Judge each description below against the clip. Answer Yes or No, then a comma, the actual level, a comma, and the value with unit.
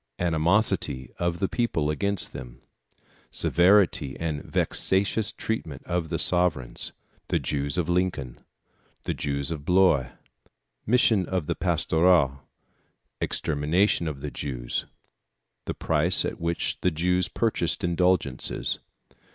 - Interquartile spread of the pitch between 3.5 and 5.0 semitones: Yes, average, 4.0 semitones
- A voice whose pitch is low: Yes, very low, 85 Hz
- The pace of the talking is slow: Yes, slow, 115 wpm